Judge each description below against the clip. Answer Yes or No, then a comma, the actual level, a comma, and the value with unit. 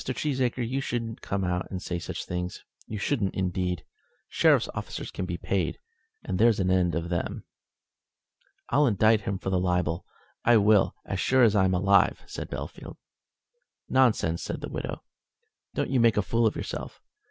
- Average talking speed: Yes, average, 165 wpm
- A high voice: No, low, 100 Hz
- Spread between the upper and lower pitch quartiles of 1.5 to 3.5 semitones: No, average, 4.3 semitones